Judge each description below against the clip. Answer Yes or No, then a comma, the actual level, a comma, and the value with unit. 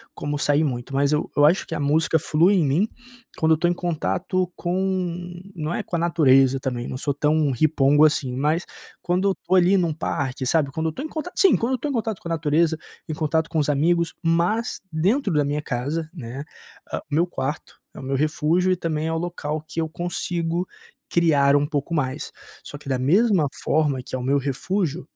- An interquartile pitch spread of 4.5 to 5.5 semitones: No, average, 3.4 semitones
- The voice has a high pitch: No, medium, 160 Hz